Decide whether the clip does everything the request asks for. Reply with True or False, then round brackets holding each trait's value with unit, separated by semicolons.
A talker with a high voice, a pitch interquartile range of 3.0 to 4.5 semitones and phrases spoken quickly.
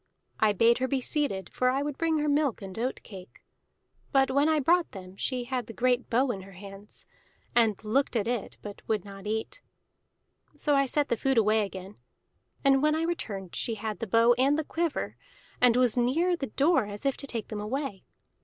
False (245 Hz; 5.0 semitones; 210 wpm)